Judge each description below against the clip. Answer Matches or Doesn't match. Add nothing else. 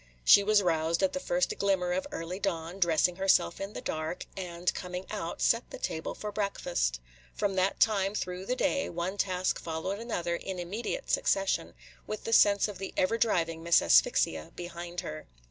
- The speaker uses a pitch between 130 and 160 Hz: Doesn't match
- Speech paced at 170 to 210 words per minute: Matches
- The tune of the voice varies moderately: Matches